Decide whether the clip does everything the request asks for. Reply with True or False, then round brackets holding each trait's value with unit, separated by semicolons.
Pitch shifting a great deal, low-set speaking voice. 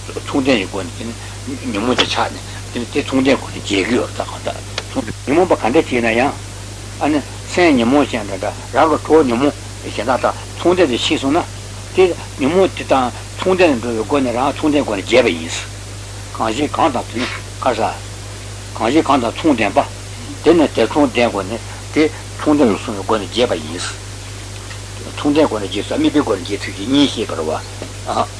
False (3.5 semitones; 105 Hz)